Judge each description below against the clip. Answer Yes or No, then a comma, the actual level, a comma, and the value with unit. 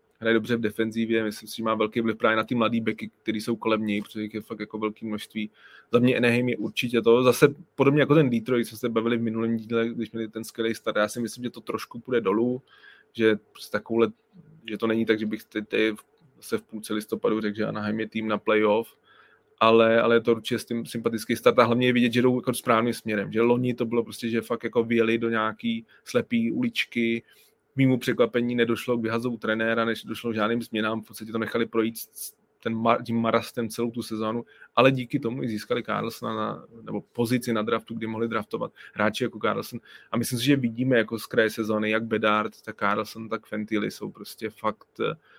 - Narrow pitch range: Yes, narrow, 1.5 semitones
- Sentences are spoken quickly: Yes, fast, 215 wpm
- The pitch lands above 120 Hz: No, low, 115 Hz